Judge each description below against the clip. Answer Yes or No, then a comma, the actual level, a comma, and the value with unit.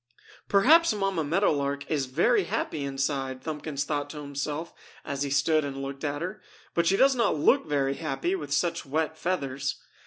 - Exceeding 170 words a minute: Yes, average, 180 wpm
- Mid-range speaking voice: Yes, medium, 150 Hz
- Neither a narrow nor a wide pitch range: Yes, average, 3.5 semitones